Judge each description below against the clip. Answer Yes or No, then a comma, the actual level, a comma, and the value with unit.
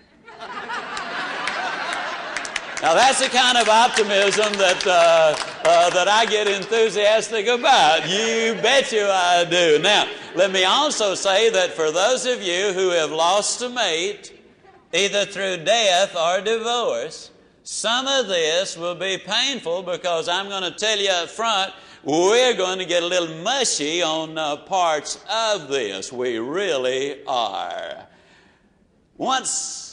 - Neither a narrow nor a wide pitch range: No, wide, 6.1 semitones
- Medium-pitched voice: No, high, 205 Hz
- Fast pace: No, slow, 135 wpm